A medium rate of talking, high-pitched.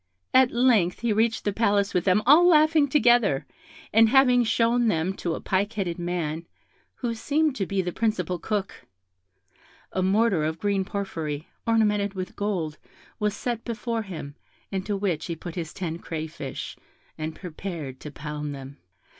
Yes: average, 160 wpm; high, 195 Hz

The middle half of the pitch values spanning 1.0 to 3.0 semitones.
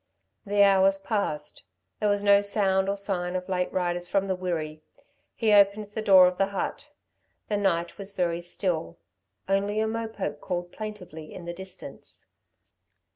Yes: narrow, 2.4 semitones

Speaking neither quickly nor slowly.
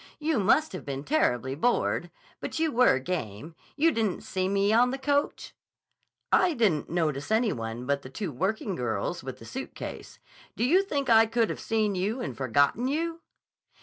Yes: average, 180 wpm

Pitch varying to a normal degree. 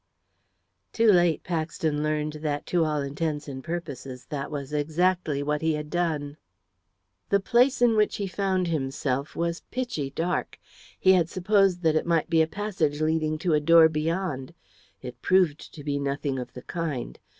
Yes: average, 3.4 semitones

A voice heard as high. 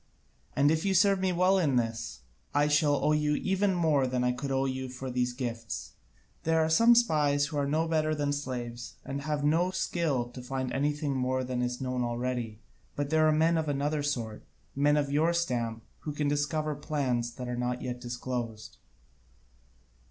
No: medium, 140 Hz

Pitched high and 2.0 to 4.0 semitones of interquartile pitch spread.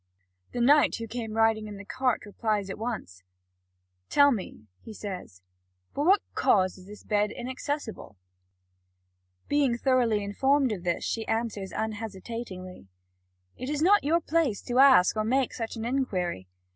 No: high, 225 Hz; average, 4.4 semitones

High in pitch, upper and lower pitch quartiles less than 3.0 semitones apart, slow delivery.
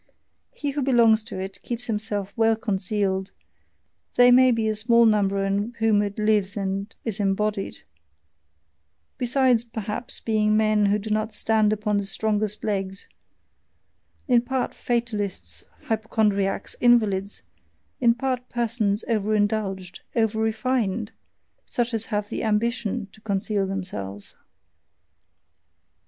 Yes: high, 215 Hz; narrow, 2.5 semitones; slow, 125 wpm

